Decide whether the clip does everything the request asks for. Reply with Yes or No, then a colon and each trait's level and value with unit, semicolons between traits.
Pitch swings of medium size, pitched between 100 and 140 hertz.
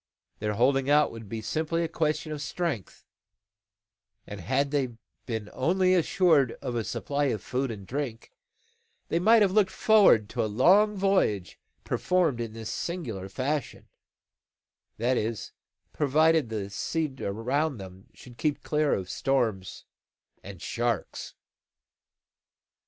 No: wide, 6.2 semitones; low, 135 Hz